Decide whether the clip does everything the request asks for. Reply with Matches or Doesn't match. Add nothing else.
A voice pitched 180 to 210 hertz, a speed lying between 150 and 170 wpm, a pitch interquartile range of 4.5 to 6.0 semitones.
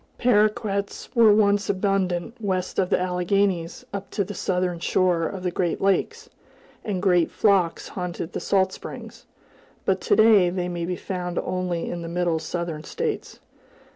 Doesn't match